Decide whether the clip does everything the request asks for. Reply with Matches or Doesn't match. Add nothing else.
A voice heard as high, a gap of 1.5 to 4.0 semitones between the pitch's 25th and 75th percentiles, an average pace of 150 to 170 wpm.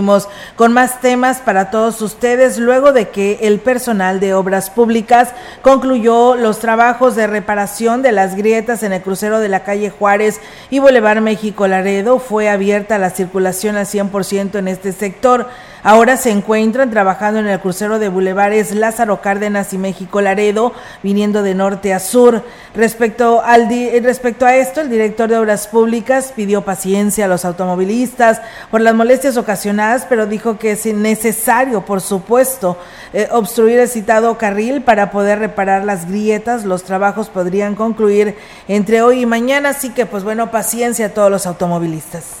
Matches